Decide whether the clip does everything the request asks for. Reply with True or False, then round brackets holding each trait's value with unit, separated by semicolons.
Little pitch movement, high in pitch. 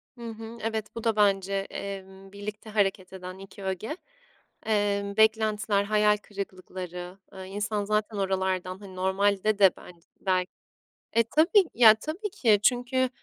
True (2.3 semitones; 205 Hz)